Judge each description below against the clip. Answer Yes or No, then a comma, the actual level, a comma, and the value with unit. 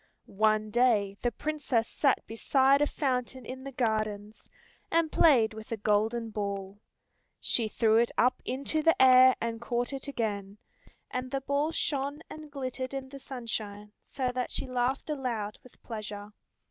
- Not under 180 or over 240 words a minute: No, average, 160 wpm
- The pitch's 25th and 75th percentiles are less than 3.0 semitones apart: No, average, 3.9 semitones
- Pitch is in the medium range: No, high, 245 Hz